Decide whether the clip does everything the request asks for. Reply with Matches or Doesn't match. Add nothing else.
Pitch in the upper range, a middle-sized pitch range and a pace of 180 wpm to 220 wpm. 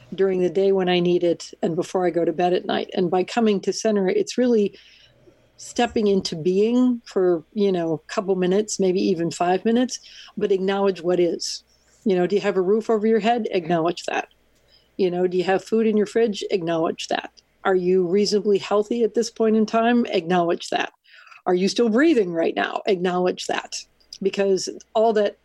Matches